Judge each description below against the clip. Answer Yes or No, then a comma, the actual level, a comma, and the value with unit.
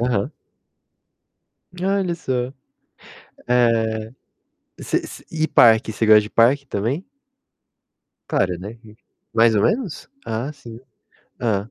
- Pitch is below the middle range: Yes, low, 115 Hz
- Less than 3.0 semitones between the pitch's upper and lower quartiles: No, average, 4.1 semitones